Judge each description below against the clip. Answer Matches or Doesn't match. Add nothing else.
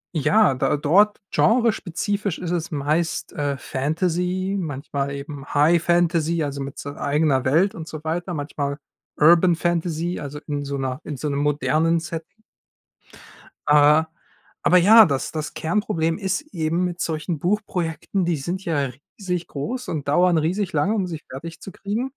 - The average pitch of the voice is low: Doesn't match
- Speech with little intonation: Doesn't match